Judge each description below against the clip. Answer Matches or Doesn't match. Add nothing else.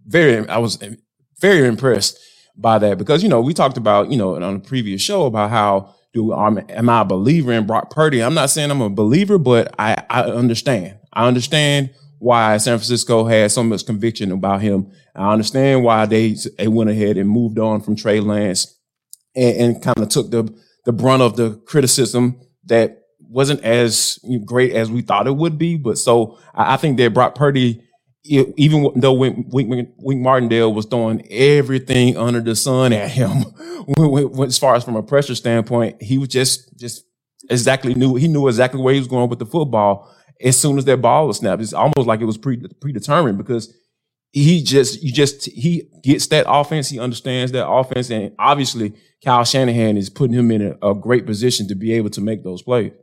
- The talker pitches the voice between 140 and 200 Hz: Doesn't match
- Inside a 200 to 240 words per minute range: Matches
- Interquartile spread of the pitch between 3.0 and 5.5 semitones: Matches